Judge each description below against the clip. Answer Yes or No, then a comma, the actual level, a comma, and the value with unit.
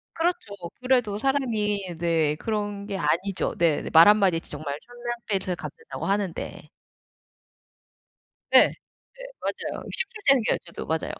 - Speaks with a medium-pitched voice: No, high, 200 Hz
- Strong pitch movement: Yes, wide, 5.9 semitones